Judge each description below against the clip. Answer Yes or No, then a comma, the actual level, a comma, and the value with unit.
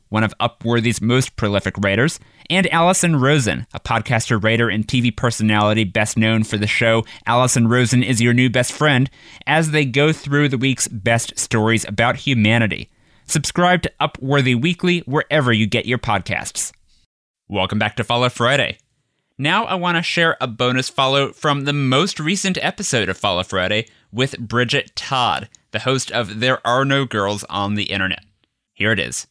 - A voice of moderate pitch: No, low, 120 Hz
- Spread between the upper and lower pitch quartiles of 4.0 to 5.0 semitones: Yes, average, 4.4 semitones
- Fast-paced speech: No, average, 170 wpm